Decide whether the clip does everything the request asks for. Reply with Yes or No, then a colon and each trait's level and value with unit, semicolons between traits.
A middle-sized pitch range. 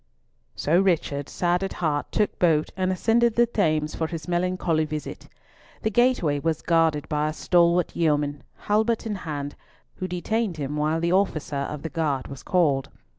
Yes: average, 3.6 semitones